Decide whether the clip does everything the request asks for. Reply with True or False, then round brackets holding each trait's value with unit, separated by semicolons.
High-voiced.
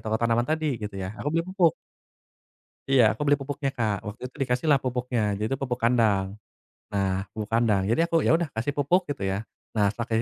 False (120 Hz)